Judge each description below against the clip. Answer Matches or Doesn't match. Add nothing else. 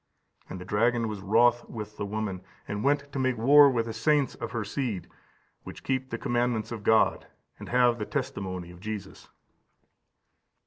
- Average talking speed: Matches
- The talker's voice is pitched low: Matches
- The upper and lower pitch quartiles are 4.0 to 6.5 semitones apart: Doesn't match